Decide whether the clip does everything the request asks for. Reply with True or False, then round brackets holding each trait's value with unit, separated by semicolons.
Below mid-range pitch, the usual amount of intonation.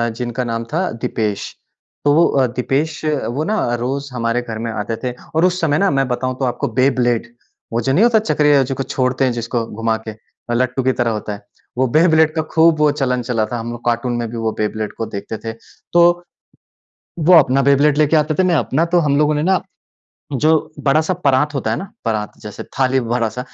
True (130 Hz; 4.6 semitones)